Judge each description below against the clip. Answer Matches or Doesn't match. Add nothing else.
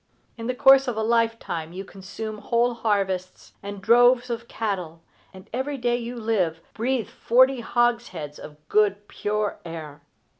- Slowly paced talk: Doesn't match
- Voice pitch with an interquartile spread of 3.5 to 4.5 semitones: Matches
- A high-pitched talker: Matches